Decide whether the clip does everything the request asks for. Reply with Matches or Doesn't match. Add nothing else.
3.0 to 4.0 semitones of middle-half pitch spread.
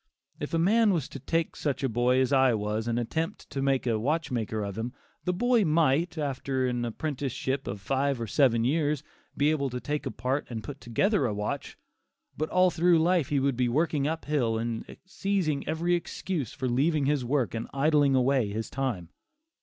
Doesn't match